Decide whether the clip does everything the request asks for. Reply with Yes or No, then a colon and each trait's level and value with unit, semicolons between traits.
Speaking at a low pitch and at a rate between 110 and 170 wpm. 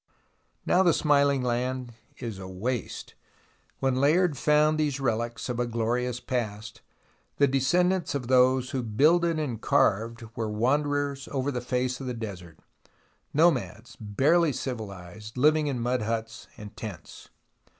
Yes: low, 125 Hz; average, 140 wpm